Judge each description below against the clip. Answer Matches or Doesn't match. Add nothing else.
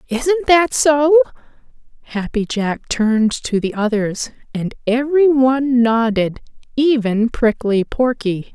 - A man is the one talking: Doesn't match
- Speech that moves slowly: Matches